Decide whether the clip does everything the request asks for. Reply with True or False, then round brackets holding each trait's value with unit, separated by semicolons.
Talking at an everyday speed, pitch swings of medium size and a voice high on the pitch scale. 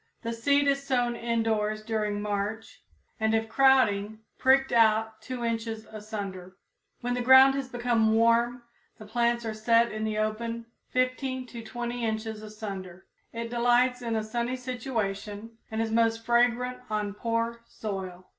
False (150 wpm; 2.1 semitones; 230 Hz)